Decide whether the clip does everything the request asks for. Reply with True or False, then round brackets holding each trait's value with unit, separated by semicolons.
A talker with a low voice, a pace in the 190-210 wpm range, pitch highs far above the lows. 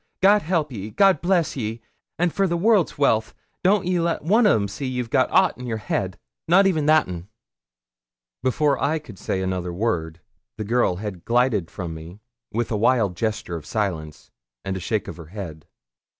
True (115 Hz; 195 wpm; 8.9 semitones)